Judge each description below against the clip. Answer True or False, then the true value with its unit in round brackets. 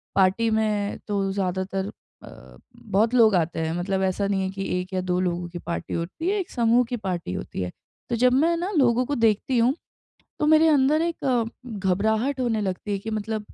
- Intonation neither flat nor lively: True (4.7 semitones)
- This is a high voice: True (210 Hz)